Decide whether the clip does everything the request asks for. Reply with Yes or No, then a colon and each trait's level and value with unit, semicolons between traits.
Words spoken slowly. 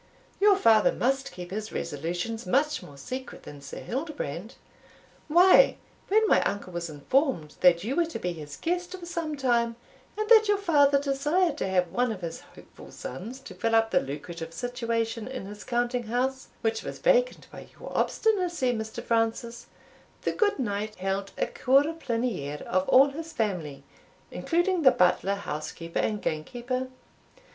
No: average, 165 wpm